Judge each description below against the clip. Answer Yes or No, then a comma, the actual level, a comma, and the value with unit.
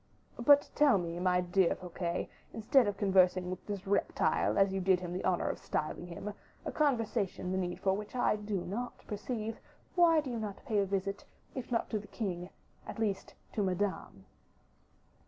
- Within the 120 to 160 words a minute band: No, average, 185 wpm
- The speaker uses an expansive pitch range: No, average, 3.4 semitones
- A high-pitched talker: Yes, high, 195 Hz